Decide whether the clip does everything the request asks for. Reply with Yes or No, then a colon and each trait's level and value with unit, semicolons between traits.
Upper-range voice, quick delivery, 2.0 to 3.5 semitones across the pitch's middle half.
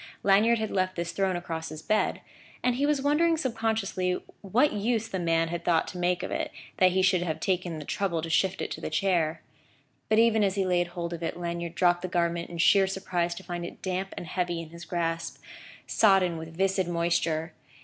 No: medium, 180 Hz; fast, 215 wpm; narrow, 2.5 semitones